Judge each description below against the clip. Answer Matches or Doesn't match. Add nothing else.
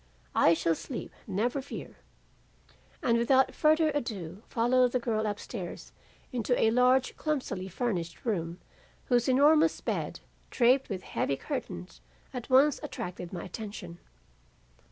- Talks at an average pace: Doesn't match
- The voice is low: Doesn't match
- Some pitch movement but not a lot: Doesn't match